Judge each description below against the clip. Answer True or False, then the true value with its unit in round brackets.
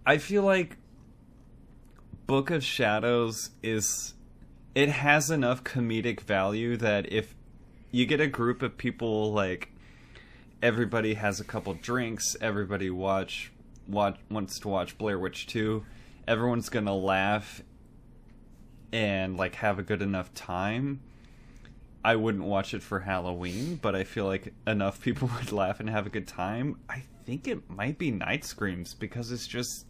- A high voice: False (115 Hz)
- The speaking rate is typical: True (150 wpm)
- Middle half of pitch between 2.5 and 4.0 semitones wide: True (3.3 semitones)